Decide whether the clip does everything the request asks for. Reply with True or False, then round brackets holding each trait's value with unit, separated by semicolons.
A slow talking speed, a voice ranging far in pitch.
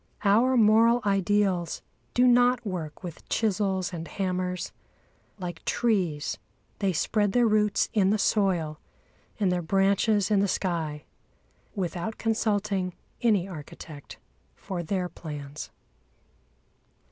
False (110 wpm; 3.4 semitones)